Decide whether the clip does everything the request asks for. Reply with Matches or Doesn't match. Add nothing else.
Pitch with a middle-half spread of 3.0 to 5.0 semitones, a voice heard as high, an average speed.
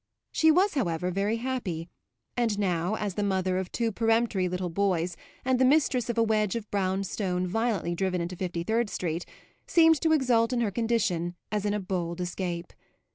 Matches